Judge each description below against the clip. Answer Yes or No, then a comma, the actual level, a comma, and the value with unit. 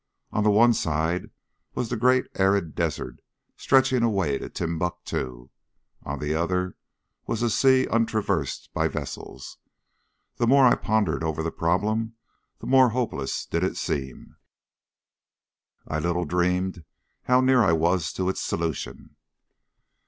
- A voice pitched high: No, very low, 90 Hz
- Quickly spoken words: No, slow, 135 wpm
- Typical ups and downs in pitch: No, wide, 6.0 semitones